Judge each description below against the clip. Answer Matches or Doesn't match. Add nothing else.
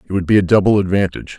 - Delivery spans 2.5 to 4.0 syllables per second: Doesn't match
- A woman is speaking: Doesn't match